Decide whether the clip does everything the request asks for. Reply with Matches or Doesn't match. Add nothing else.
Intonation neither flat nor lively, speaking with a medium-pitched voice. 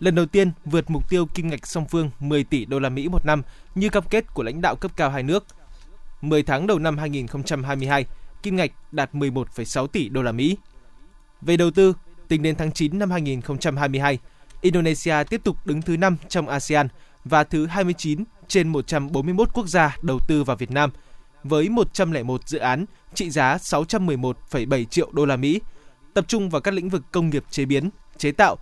Matches